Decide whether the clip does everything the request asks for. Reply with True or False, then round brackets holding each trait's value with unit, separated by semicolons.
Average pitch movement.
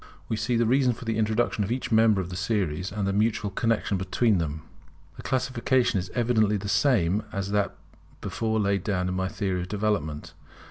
True (3.4 semitones)